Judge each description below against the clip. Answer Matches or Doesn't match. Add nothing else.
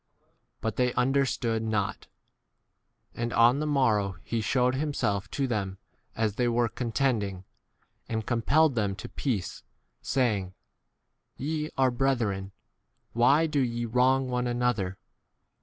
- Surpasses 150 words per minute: Doesn't match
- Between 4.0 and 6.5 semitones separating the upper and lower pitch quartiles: Doesn't match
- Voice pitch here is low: Matches